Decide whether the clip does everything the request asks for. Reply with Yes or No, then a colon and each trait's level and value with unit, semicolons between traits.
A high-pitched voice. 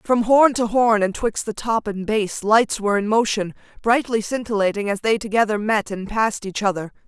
Yes: high, 215 Hz